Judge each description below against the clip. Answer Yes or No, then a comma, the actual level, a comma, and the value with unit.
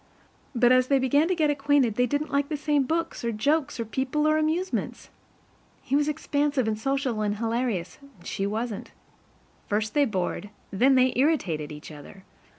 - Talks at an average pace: Yes, average, 180 wpm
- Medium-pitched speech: No, very high, 260 Hz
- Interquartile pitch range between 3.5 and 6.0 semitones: Yes, average, 5.2 semitones